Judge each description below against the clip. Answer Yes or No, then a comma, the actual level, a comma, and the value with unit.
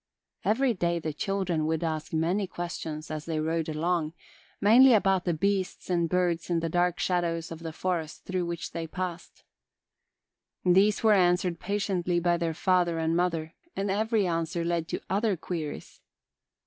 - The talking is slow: No, average, 160 wpm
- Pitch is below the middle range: No, medium, 175 Hz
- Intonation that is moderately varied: No, narrow, 2.3 semitones